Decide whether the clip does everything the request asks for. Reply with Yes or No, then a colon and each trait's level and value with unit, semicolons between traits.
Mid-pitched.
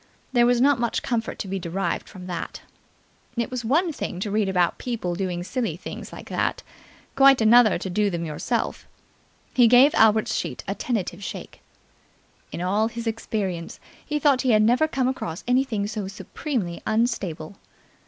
No: high, 220 Hz